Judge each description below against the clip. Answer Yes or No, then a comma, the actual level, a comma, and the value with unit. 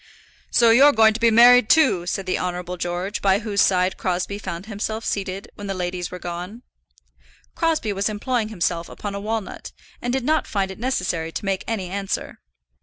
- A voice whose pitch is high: Yes, high, 200 Hz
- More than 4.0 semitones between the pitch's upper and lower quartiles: No, average, 3.7 semitones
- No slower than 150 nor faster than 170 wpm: No, average, 185 wpm